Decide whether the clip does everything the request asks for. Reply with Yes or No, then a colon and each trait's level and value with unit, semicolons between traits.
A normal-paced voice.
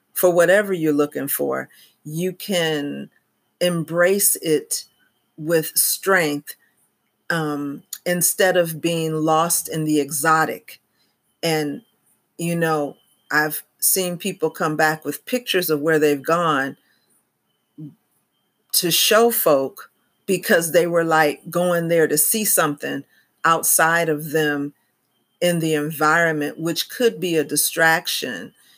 No: slow, 115 wpm